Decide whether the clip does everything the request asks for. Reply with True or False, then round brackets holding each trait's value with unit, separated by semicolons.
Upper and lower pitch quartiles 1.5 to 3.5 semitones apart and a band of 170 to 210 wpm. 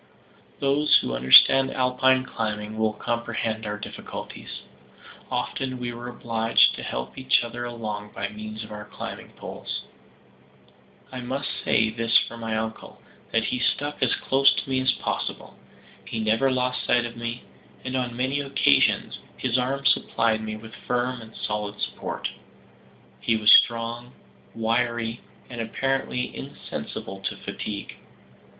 False (2.6 semitones; 145 wpm)